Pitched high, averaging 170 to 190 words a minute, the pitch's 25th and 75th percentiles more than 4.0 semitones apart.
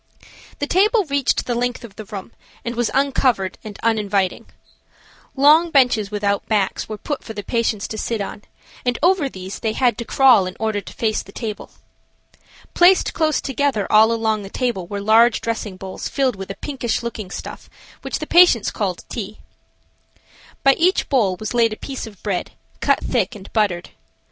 Yes: high, 225 Hz; average, 180 wpm; average, 4.4 semitones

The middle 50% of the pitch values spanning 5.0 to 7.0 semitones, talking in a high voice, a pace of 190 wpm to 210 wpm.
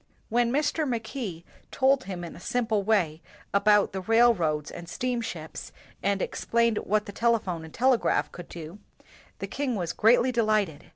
No: average, 5.3 semitones; high, 215 Hz; average, 155 wpm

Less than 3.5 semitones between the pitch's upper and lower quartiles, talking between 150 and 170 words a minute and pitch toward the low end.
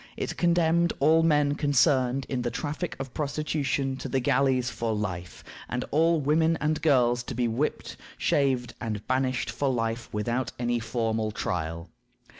No: average, 3.9 semitones; average, 155 wpm; low, 130 Hz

